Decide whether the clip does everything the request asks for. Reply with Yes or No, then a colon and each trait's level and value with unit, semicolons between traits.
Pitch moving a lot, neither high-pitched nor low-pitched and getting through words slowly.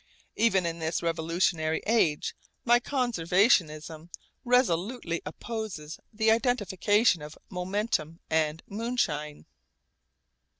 Yes: wide, 5.9 semitones; medium, 180 Hz; slow, 85 wpm